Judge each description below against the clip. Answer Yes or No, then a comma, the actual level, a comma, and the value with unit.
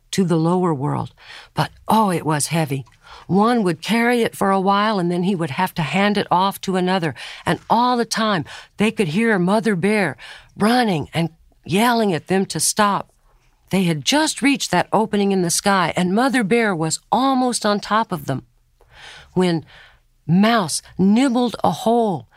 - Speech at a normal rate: Yes, average, 175 wpm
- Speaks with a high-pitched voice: Yes, high, 195 Hz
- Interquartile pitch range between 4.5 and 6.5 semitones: Yes, average, 4.8 semitones